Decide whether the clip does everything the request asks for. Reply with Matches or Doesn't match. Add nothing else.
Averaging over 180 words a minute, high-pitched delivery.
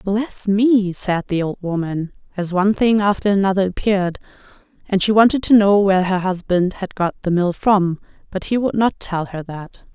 Matches